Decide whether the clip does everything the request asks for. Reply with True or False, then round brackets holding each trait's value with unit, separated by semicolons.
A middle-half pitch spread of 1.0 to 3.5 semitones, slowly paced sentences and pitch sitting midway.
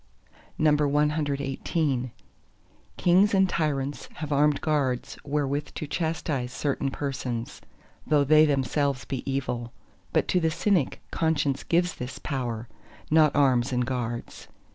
True (2.9 semitones; 115 wpm; 145 Hz)